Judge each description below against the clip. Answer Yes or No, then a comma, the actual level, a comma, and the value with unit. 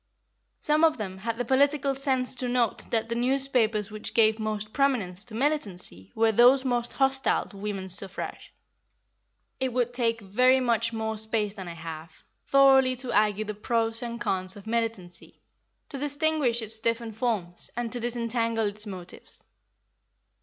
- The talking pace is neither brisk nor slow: Yes, average, 160 wpm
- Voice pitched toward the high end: Yes, high, 230 Hz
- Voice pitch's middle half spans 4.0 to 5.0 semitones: No, average, 3.3 semitones